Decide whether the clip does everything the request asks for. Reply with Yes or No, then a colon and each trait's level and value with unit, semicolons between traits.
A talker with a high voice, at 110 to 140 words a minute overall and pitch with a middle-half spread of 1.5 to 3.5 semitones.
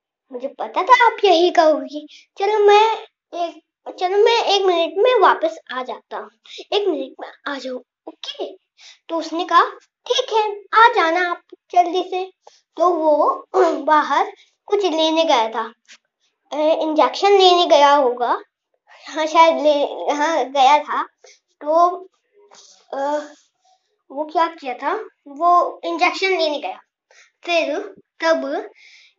No: very high, 345 Hz; average, 130 wpm; average, 4.6 semitones